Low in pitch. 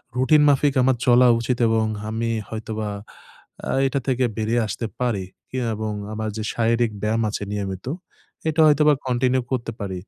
Yes: low, 115 Hz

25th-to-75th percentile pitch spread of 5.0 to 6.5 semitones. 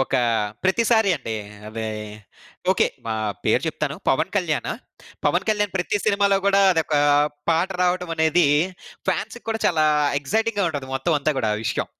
Yes: average, 5.3 semitones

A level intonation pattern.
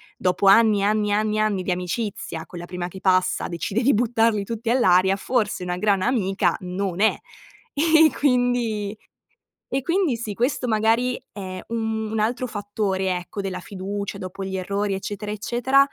No: average, 3.4 semitones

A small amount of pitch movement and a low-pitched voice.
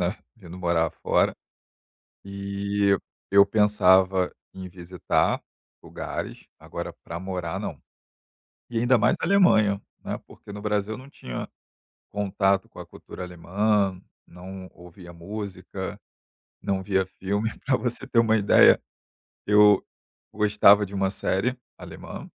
Yes: narrow, 2.2 semitones; low, 100 Hz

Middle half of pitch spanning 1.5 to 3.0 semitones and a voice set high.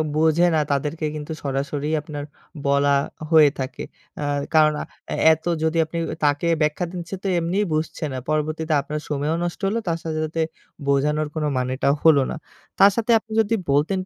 No: narrow, 2.4 semitones; medium, 155 Hz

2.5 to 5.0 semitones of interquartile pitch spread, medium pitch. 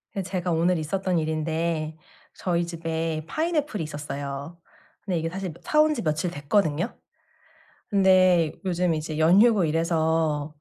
Yes: average, 3.0 semitones; medium, 165 Hz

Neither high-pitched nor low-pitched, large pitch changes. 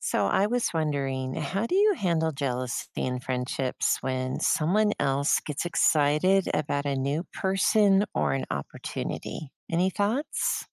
Yes: medium, 150 Hz; wide, 6.5 semitones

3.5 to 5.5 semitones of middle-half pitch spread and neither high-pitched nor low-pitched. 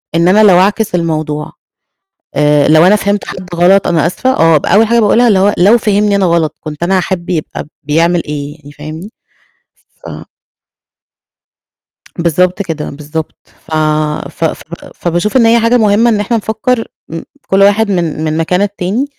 Yes: average, 4.5 semitones; medium, 180 Hz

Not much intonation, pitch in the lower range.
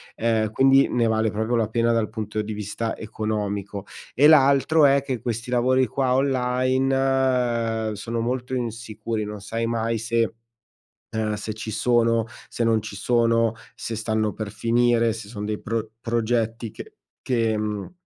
Yes: narrow, 2.1 semitones; low, 115 Hz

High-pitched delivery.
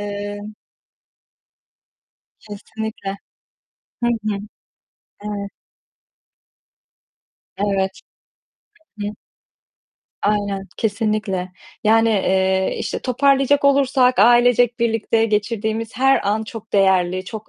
Yes: high, 215 Hz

